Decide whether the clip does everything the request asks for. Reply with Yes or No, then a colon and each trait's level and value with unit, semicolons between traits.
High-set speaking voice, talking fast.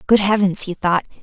No: high, 195 Hz; average, 195 wpm